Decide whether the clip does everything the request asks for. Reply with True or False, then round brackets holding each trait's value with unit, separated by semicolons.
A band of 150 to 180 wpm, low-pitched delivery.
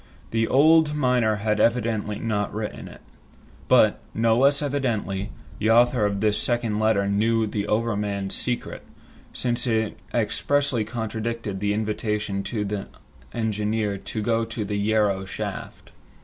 False (135 wpm; 110 Hz)